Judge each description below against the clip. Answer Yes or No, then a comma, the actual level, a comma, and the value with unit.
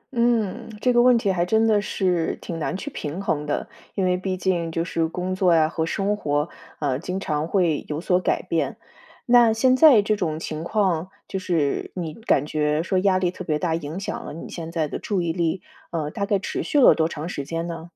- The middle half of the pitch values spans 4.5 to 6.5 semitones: No, average, 3.7 semitones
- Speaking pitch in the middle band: Yes, medium, 180 Hz